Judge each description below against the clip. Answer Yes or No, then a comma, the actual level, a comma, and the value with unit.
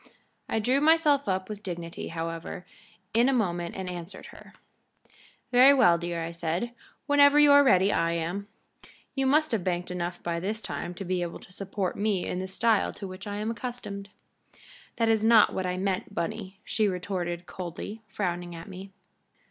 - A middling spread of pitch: Yes, average, 4.3 semitones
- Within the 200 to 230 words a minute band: No, average, 180 wpm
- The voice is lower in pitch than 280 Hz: Yes, high, 190 Hz